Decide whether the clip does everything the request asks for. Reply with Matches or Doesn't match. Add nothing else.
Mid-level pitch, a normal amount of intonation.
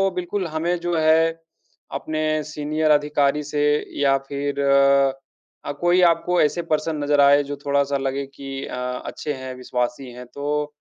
Doesn't match